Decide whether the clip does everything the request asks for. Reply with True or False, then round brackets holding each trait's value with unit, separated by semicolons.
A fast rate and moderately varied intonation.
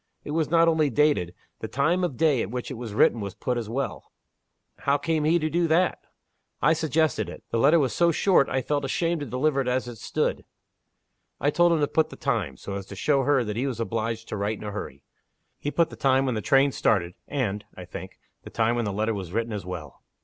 False (245 wpm; 5.8 semitones)